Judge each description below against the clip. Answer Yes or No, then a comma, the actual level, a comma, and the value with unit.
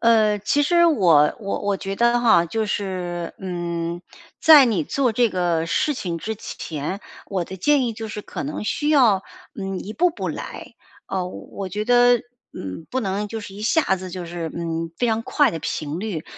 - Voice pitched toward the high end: Yes, high, 200 Hz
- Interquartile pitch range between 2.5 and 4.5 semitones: No, wide, 5.4 semitones